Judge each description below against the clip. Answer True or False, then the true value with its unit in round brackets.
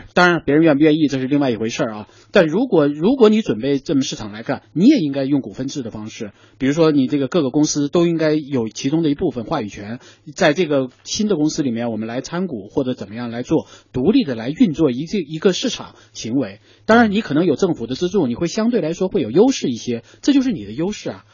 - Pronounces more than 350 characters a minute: True (370 characters per minute)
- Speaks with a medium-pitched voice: True (150 Hz)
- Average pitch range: False (6.4 semitones)